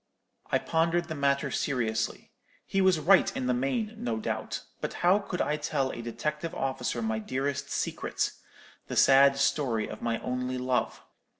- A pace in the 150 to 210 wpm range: Yes, average, 160 wpm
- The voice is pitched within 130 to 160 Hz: Yes, medium, 140 Hz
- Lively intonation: No, average, 4.1 semitones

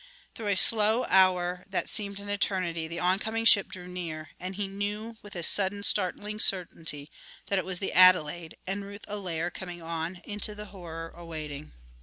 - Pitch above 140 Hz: Yes, medium, 185 Hz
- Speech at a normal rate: Yes, average, 180 wpm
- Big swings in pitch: No, average, 3.0 semitones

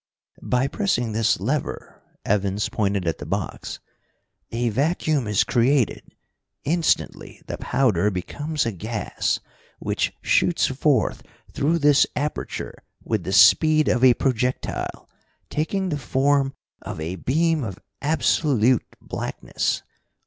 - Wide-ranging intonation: Yes, wide, 6.0 semitones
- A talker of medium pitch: No, low, 125 Hz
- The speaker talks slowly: Yes, slow, 120 wpm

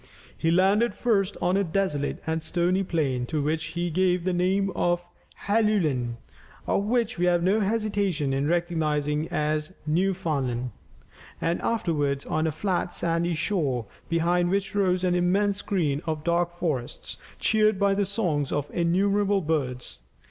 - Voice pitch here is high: No, medium, 175 Hz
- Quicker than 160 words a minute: No, average, 150 wpm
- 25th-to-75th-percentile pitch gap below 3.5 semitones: No, average, 4.2 semitones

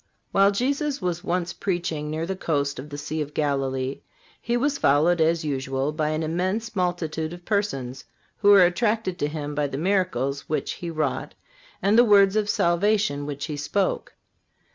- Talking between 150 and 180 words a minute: Yes, average, 175 wpm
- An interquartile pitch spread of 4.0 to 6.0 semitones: Yes, average, 5.2 semitones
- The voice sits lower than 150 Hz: No, medium, 170 Hz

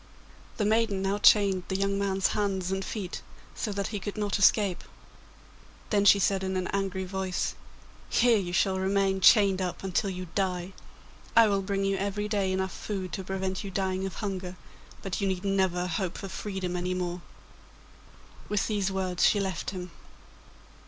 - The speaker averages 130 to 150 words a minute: No, average, 175 wpm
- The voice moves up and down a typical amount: No, narrow, 1.3 semitones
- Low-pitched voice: No, high, 195 Hz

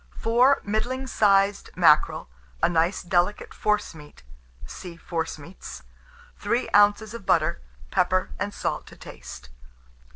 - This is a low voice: No, high, 195 Hz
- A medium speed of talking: No, slow, 110 wpm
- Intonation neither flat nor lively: Yes, average, 4.2 semitones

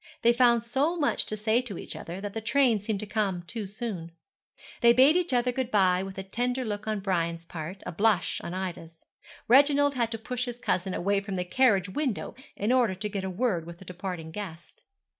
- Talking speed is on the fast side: Yes, fast, 215 wpm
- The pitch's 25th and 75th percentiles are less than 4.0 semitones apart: No, average, 4.7 semitones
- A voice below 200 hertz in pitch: No, high, 210 Hz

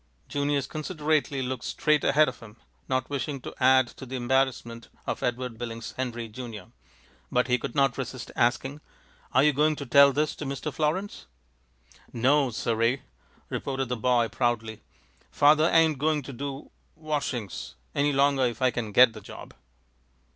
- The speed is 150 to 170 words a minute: Yes, average, 160 wpm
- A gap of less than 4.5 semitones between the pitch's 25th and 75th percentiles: Yes, average, 3.2 semitones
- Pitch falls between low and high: No, low, 130 Hz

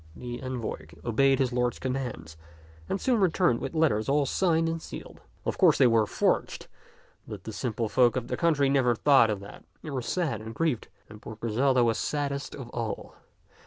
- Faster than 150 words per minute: Yes, average, 190 wpm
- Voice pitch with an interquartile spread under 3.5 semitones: No, average, 4.0 semitones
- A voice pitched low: Yes, low, 130 Hz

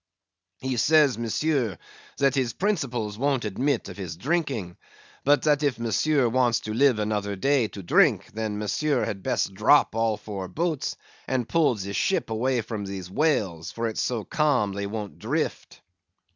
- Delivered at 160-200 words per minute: Yes, average, 165 wpm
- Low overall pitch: Yes, low, 115 Hz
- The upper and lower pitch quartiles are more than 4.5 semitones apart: Yes, average, 5.3 semitones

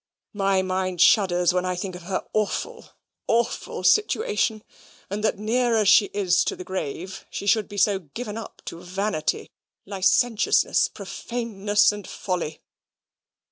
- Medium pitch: No, high, 200 Hz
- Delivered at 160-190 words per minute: No, average, 140 wpm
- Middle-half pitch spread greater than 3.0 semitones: No, average, 2.7 semitones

